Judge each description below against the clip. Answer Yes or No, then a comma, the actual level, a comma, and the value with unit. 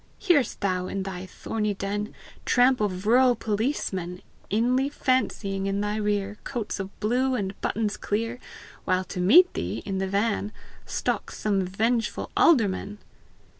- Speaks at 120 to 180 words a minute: Yes, average, 140 wpm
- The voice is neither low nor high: No, high, 210 Hz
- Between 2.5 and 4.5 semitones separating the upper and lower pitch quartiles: Yes, average, 3.6 semitones